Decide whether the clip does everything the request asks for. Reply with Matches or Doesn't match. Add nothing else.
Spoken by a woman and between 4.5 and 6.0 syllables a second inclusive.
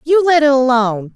Matches